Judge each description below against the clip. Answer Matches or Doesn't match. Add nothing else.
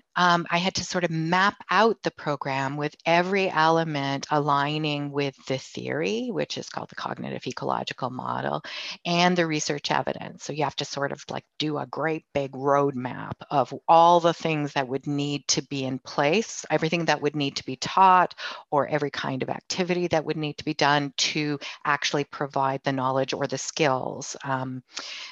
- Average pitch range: Matches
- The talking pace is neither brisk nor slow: Matches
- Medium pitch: Matches